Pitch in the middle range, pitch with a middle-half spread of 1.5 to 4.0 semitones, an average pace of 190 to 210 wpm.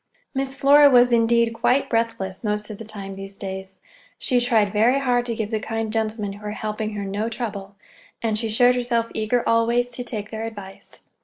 No: high, 225 Hz; narrow, 2.5 semitones; average, 200 wpm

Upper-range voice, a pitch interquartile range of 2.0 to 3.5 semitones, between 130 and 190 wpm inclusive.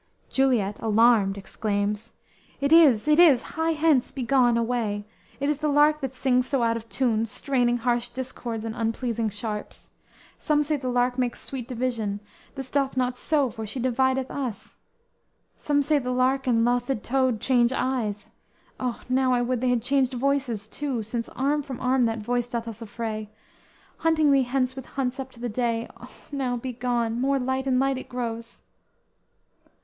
Yes: very high, 250 Hz; narrow, 2.6 semitones; average, 175 wpm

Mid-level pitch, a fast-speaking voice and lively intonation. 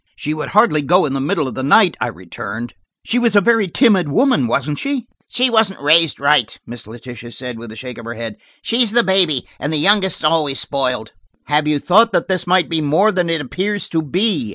Yes: medium, 155 Hz; fast, 225 wpm; wide, 7.2 semitones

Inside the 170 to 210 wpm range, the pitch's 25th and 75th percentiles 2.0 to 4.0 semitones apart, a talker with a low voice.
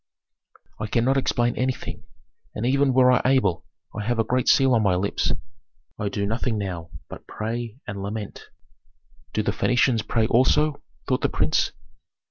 No: average, 160 wpm; average, 3.5 semitones; low, 115 Hz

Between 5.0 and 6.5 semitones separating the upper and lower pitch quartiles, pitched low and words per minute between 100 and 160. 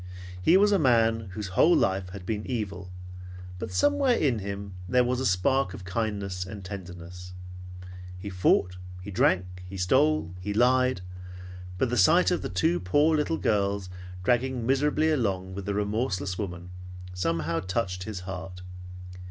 Yes: wide, 5.4 semitones; low, 100 Hz; average, 150 wpm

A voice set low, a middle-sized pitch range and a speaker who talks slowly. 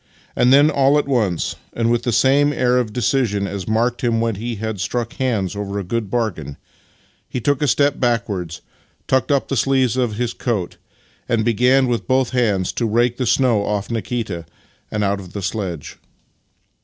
No: low, 115 Hz; average, 3.8 semitones; average, 185 wpm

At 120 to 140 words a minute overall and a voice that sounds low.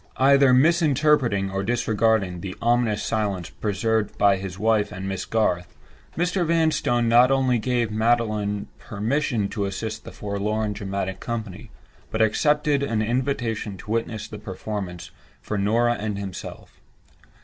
Yes: slow, 135 wpm; low, 110 Hz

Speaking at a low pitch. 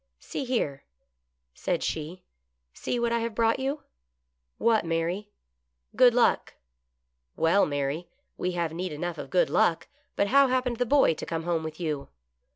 No: medium, 170 Hz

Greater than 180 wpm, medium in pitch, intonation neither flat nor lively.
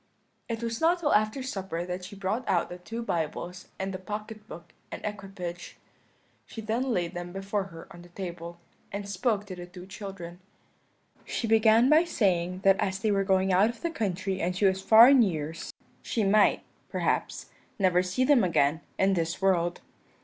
No: average, 190 wpm; high, 195 Hz; average, 3.5 semitones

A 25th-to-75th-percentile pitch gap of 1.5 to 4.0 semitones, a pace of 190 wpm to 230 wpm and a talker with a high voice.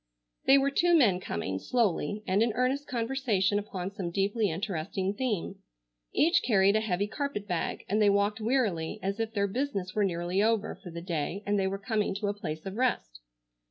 Yes: average, 3.3 semitones; average, 195 wpm; high, 205 Hz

